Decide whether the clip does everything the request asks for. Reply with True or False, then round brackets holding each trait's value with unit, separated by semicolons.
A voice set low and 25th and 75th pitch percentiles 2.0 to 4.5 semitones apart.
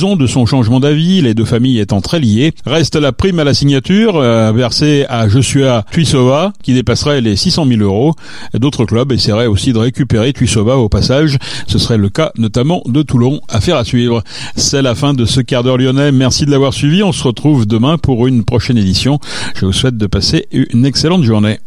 True (130 Hz; 3.8 semitones)